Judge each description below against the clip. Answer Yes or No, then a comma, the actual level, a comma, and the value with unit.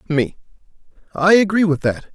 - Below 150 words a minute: Yes, average, 140 wpm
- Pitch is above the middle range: No, medium, 170 Hz